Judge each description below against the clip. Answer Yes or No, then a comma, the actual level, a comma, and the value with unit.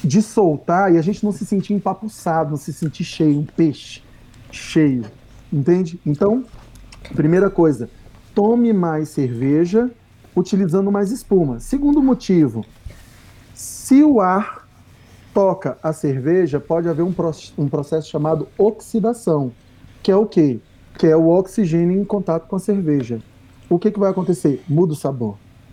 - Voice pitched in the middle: Yes, medium, 165 Hz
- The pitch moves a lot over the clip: Yes, wide, 7.0 semitones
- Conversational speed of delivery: Yes, average, 145 wpm